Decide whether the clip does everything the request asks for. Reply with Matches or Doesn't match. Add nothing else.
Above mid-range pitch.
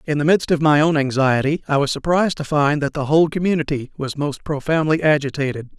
Doesn't match